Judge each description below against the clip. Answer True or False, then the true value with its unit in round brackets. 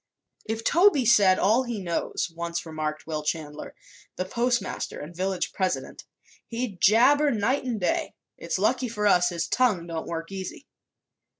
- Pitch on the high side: True (195 Hz)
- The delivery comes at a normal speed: True (155 wpm)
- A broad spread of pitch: True (5.9 semitones)